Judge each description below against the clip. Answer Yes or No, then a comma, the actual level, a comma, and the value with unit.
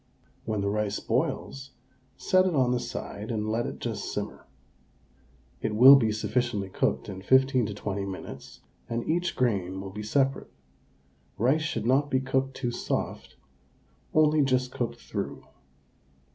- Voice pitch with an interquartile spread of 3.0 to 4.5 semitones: Yes, average, 4.1 semitones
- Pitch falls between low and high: No, low, 120 Hz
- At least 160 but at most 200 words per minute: No, average, 150 wpm